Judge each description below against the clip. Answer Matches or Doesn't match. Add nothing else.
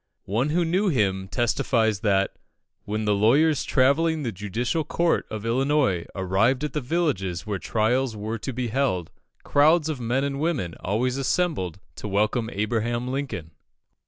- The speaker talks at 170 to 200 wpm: Doesn't match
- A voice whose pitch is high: Doesn't match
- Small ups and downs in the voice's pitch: Doesn't match